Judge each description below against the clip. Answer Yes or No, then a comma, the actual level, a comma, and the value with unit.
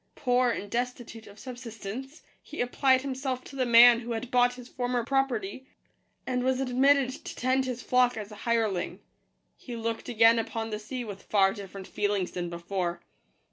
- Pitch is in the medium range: No, high, 240 Hz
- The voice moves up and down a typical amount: Yes, average, 3.1 semitones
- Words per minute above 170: Yes, average, 180 wpm